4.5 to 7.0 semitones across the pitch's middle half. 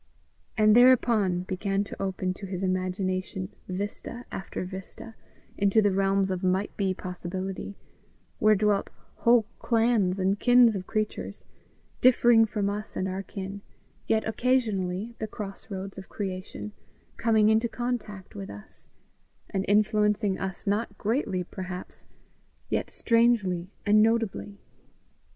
No: narrow, 2.6 semitones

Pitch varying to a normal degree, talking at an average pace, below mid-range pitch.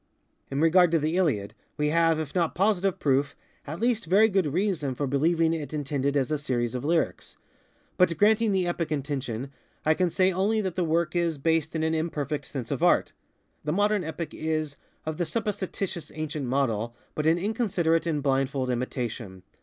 No: average, 4.1 semitones; average, 185 wpm; medium, 160 Hz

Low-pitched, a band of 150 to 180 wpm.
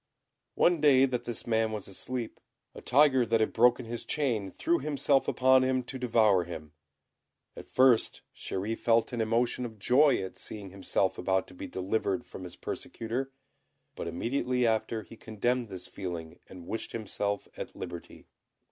Yes: low, 115 Hz; average, 165 wpm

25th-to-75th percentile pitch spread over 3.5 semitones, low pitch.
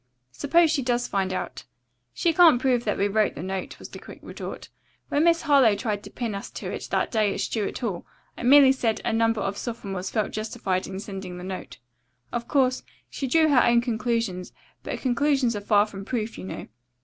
No: average, 4.5 semitones; high, 230 Hz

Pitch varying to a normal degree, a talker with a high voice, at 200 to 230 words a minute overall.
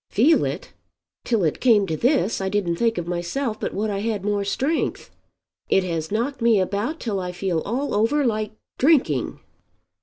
No: average, 4.3 semitones; high, 210 Hz; average, 180 wpm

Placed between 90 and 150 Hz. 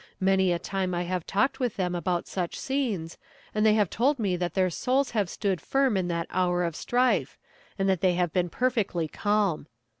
No: high, 190 Hz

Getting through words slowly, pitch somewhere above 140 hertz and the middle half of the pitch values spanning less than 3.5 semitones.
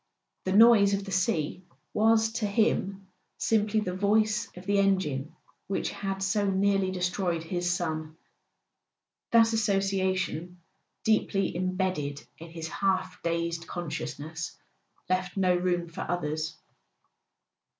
Yes: slow, 120 wpm; medium, 185 Hz; average, 2.9 semitones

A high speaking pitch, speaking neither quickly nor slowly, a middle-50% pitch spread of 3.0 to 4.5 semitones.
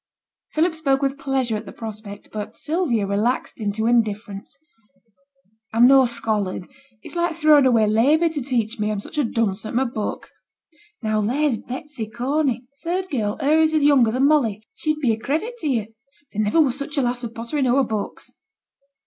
No: high, 245 Hz; average, 185 wpm; average, 5.2 semitones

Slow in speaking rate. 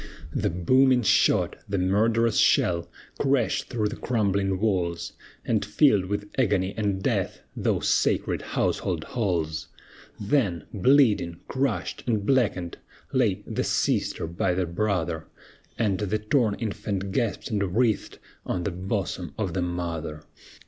Yes: slow, 130 wpm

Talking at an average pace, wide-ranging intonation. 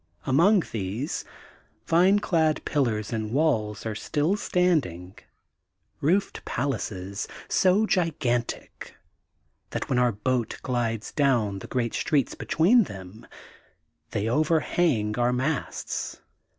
No: slow, 100 wpm; wide, 7.0 semitones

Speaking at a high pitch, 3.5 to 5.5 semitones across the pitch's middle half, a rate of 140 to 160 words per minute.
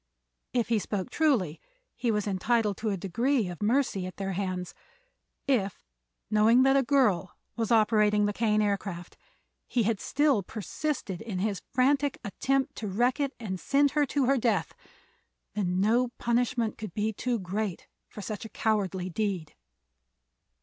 Yes: high, 215 Hz; average, 4.2 semitones; average, 155 wpm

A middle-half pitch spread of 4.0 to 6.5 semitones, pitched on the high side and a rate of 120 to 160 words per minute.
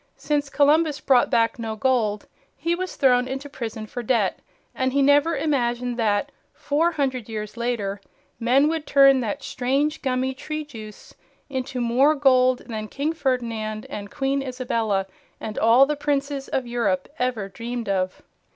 No: average, 3.6 semitones; very high, 255 Hz; average, 155 wpm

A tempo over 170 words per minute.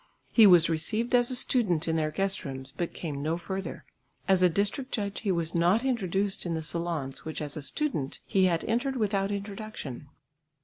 Yes: average, 190 wpm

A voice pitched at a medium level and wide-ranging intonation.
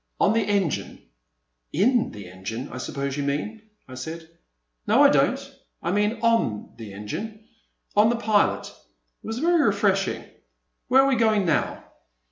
No: high, 205 Hz; wide, 8.2 semitones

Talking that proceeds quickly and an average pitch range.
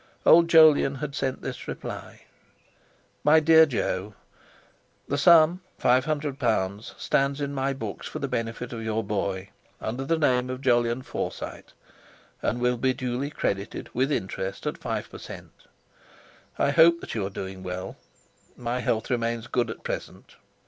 No: average, 150 wpm; average, 4.1 semitones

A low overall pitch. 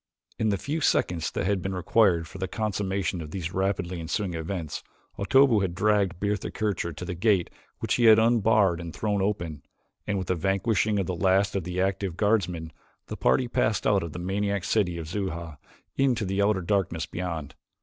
Yes: very low, 95 Hz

